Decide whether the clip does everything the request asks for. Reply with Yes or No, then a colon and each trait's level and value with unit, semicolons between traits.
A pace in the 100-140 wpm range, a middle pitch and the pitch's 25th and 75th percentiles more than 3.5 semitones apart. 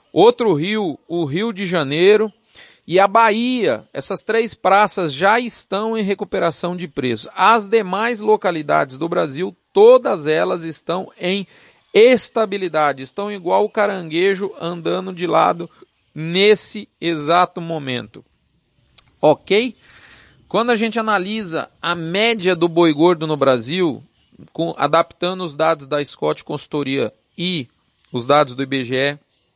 Yes: average, 125 wpm; medium, 180 Hz; average, 4.8 semitones